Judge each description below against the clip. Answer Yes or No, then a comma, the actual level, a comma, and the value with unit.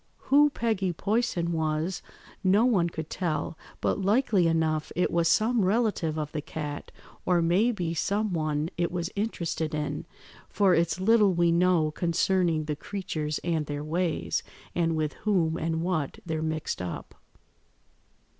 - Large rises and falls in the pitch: No, average, 3.4 semitones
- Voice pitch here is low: No, medium, 170 Hz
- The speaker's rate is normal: Yes, average, 150 wpm